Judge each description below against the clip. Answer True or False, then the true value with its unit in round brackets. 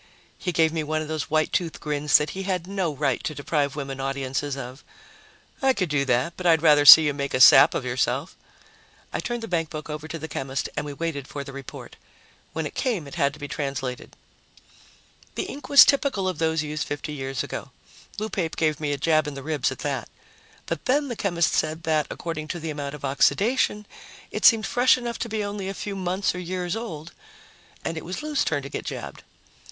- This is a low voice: False (155 Hz)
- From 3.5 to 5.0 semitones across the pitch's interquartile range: True (4.6 semitones)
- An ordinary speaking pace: False (220 wpm)